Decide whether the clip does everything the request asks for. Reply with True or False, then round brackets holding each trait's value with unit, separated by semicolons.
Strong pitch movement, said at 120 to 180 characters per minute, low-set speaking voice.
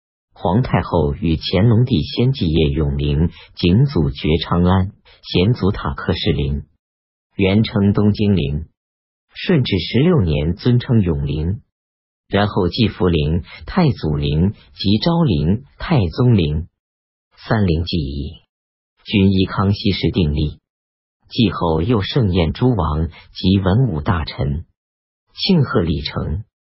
True (6.0 semitones; 175 characters per minute; 85 Hz)